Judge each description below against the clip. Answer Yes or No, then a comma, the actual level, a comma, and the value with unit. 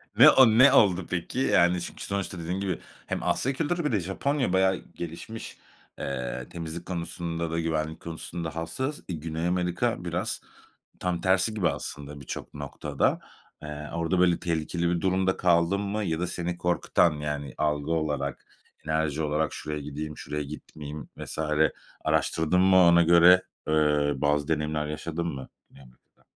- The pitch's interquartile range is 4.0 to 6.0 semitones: No, average, 3.2 semitones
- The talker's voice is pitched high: No, very low, 85 Hz